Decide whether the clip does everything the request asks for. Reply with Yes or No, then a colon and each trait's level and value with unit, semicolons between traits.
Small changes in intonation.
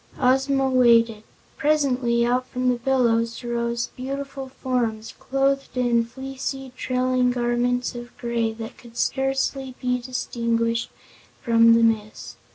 Yes: narrow, 2.1 semitones